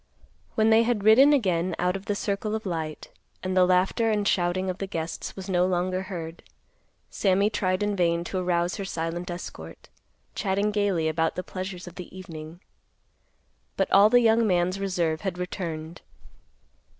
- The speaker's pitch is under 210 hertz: Yes, medium, 185 Hz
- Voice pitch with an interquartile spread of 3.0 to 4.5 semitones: No, narrow, 2.6 semitones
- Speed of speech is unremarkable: Yes, average, 170 wpm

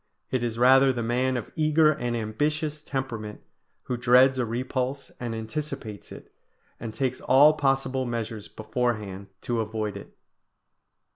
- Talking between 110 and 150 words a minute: Yes, average, 140 wpm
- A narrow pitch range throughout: No, average, 3.0 semitones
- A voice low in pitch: Yes, low, 125 Hz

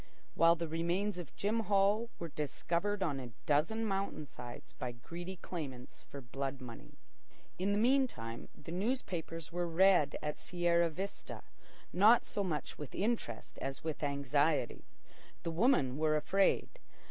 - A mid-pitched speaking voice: Yes, medium, 170 Hz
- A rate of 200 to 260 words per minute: No, average, 145 wpm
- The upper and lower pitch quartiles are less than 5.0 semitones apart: No, wide, 5.4 semitones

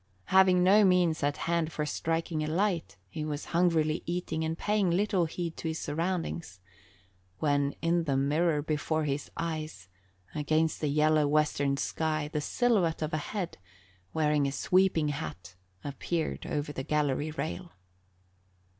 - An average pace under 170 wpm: Yes, average, 145 wpm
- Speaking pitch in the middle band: Yes, medium, 155 Hz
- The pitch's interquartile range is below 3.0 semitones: Yes, narrow, 2.6 semitones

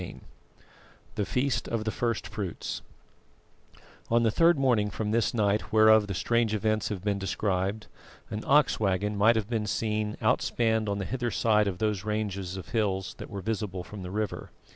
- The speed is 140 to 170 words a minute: No, average, 185 wpm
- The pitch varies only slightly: Yes, narrow, 2.0 semitones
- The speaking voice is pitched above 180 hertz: No, low, 105 Hz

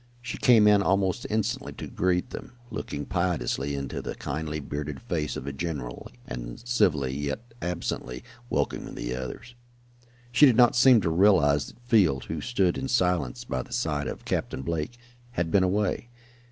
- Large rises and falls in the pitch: Yes, wide, 7.1 semitones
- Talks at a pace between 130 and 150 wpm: No, average, 165 wpm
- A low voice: Yes, very low, 85 Hz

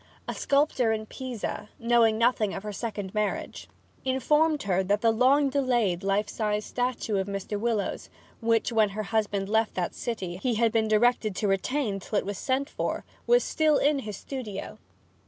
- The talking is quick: No, average, 175 wpm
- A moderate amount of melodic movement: Yes, average, 3.8 semitones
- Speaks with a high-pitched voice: Yes, high, 220 Hz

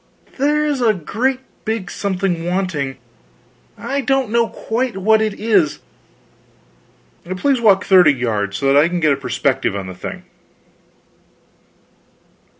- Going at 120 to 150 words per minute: Yes, average, 140 wpm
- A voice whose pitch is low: No, high, 190 Hz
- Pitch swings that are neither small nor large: No, wide, 8.1 semitones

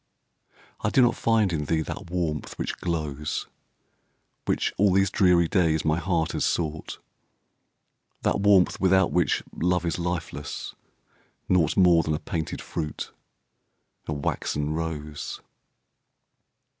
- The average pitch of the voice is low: Yes, very low, 85 Hz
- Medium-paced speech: No, slow, 125 wpm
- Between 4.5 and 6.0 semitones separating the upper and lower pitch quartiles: No, average, 2.8 semitones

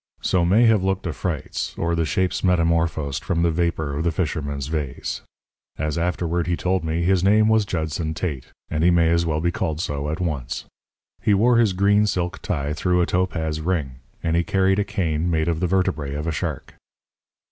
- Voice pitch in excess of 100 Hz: No, very low, 85 Hz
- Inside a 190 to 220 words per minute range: Yes, average, 200 wpm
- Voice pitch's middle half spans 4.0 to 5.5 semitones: No, average, 2.9 semitones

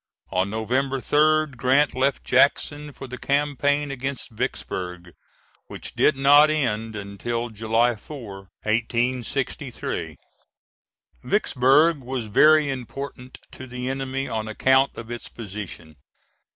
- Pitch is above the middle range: No, low, 125 Hz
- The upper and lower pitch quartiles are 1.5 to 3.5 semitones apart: No, average, 3.9 semitones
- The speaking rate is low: Yes, slow, 110 wpm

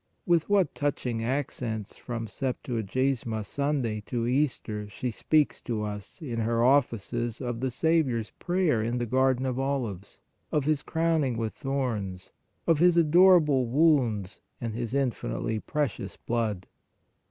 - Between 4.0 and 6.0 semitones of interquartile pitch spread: Yes, average, 4.3 semitones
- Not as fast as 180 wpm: Yes, average, 140 wpm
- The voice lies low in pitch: Yes, low, 125 Hz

